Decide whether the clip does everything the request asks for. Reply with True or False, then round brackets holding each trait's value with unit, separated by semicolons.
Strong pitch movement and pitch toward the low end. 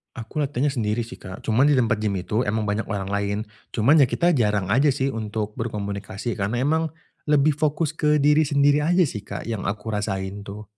True (5.8 semitones; 115 Hz)